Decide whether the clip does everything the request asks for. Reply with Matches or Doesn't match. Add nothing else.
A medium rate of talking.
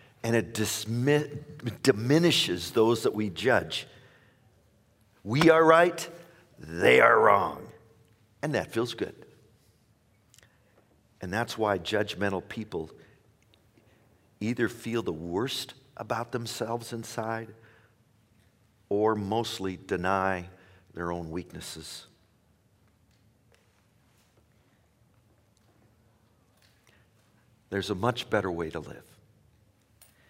Doesn't match